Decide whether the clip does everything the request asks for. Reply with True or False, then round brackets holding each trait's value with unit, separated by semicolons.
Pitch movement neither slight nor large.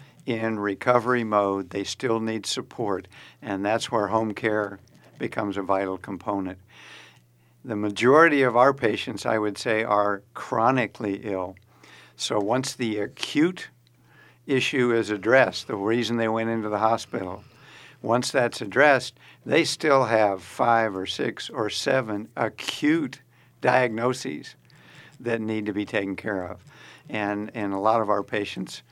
True (3.0 semitones)